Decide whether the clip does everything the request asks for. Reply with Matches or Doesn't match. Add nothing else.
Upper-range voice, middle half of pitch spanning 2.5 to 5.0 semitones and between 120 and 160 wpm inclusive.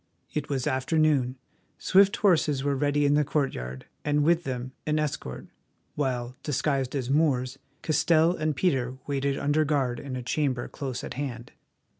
Doesn't match